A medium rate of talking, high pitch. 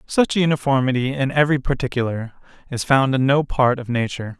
No: average, 180 wpm; low, 130 Hz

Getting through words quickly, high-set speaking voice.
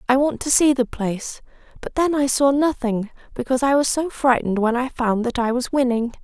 Yes: fast, 220 wpm; very high, 255 Hz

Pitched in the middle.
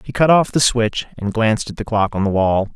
No: low, 115 Hz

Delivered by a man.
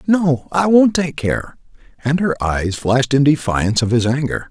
Yes: male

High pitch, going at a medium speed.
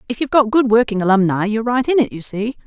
No: high, 230 Hz; fast, 270 wpm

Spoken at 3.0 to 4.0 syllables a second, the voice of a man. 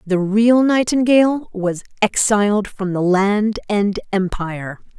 No: 3.9 syllables/s; female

